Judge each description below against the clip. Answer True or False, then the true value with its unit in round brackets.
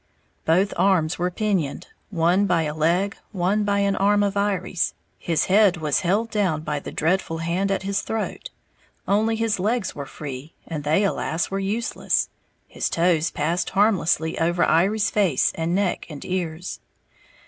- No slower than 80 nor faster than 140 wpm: False (160 wpm)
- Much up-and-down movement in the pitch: False (3.7 semitones)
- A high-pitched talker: False (180 Hz)